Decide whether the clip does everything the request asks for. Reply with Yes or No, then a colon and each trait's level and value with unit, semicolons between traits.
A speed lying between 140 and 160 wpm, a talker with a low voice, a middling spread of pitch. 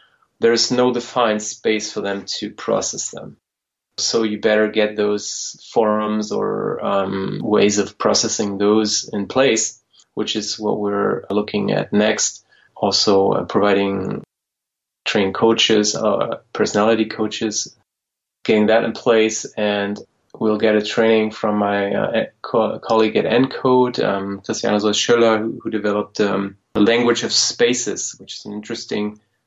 No: average, 145 wpm; low, 105 Hz; narrow, 1.4 semitones